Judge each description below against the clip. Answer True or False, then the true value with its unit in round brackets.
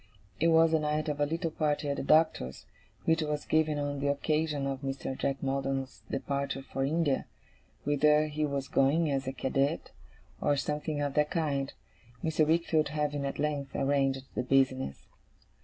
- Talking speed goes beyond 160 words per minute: True (170 wpm)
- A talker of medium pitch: True (145 Hz)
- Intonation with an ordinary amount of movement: False (2.0 semitones)